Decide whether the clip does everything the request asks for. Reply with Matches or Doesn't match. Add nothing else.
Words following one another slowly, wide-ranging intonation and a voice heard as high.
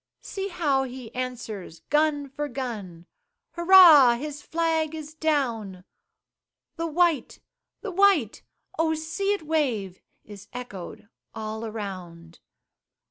Matches